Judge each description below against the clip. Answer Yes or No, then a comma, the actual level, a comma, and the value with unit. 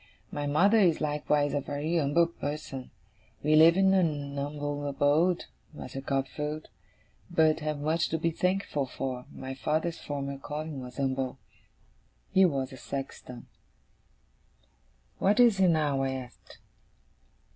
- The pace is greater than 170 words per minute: No, slow, 135 wpm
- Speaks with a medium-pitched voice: Yes, medium, 145 Hz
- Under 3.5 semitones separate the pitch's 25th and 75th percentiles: Yes, average, 3.1 semitones